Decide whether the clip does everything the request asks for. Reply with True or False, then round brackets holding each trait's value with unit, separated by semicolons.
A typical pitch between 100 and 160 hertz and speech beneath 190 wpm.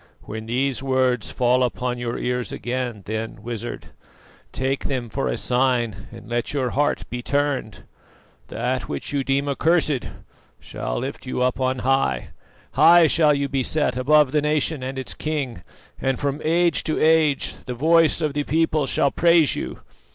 True (135 Hz; 165 wpm)